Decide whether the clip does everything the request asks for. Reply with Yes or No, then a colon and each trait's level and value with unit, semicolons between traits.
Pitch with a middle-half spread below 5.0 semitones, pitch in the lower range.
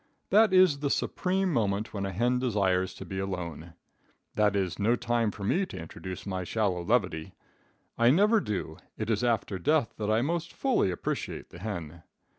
No: average, 5.3 semitones; low, 105 Hz